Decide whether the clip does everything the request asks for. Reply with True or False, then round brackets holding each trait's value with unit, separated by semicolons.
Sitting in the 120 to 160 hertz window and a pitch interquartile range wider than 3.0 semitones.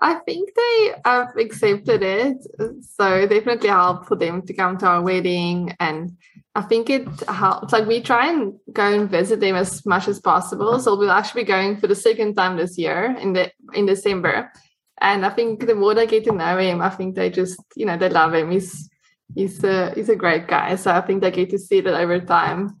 False (195 Hz; 3.5 semitones)